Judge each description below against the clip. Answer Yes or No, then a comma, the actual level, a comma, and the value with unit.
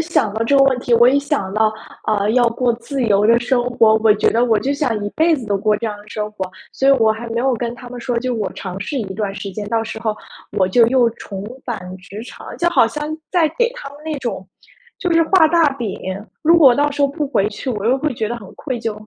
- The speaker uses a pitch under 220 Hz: No, high, 235 Hz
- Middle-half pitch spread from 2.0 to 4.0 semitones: No, average, 4.5 semitones